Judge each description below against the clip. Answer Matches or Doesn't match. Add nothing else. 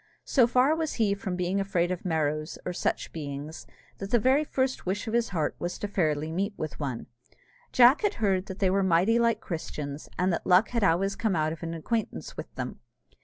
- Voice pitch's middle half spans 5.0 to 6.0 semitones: Matches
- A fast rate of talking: Matches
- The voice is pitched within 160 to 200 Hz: Matches